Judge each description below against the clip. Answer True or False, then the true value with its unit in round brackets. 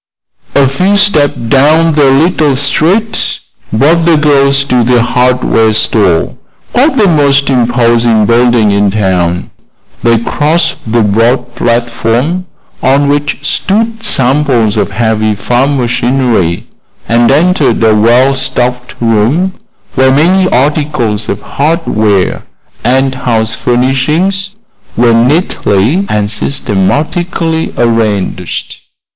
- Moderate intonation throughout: True (4.7 semitones)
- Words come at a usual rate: False (110 wpm)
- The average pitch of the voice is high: False (130 Hz)